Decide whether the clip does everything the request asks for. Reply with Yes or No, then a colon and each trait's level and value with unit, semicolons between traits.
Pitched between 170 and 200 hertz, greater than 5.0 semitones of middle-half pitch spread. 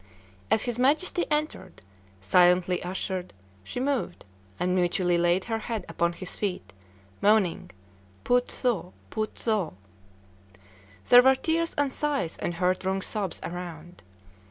Yes: high, 190 Hz; wide, 5.6 semitones